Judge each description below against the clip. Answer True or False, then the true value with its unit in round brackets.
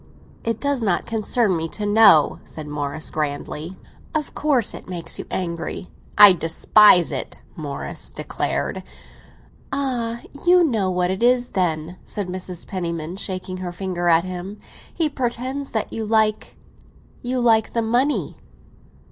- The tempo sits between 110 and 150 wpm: True (140 wpm)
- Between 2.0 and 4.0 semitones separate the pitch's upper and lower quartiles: False (5.3 semitones)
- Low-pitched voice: False (195 Hz)